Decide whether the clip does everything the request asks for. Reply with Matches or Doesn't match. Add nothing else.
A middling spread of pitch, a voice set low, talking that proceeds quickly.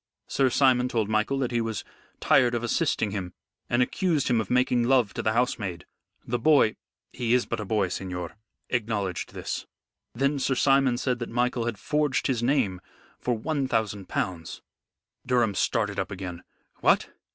Doesn't match